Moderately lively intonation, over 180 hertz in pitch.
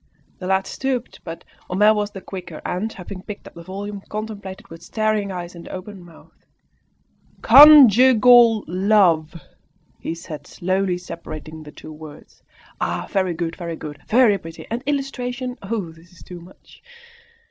Yes: average, 4.2 semitones; high, 190 Hz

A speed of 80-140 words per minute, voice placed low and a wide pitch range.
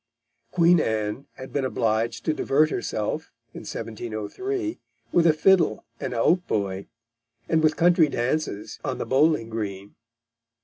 Yes: slow, 135 wpm; low, 130 Hz; wide, 6.7 semitones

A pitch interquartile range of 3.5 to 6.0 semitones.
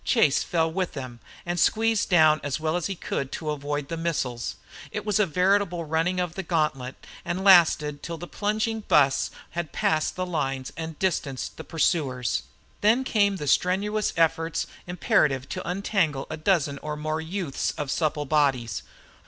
Yes: average, 3.8 semitones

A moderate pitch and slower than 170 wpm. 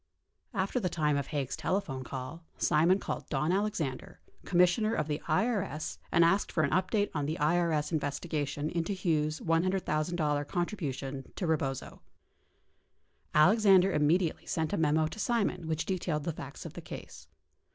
Yes: medium, 160 Hz; average, 160 wpm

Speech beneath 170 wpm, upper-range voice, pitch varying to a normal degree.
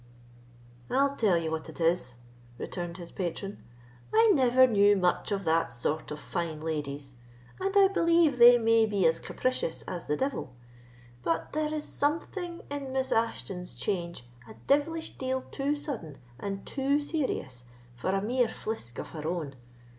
No: average, 160 wpm; high, 205 Hz; wide, 9.0 semitones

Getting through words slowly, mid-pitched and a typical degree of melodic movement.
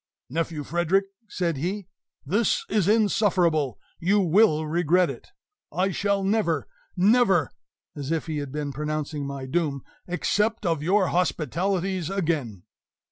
Yes: slow, 130 wpm; medium, 175 Hz; average, 4.4 semitones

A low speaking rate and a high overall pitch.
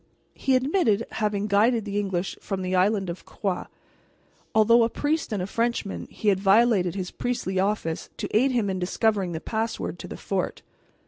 No: average, 180 wpm; high, 205 Hz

